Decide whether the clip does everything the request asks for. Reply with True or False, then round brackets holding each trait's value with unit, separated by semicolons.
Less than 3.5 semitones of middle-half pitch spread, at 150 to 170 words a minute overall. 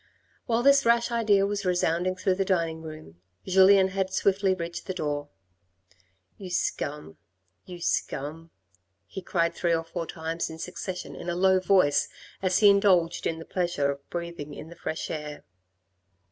True (2.9 semitones; 165 wpm)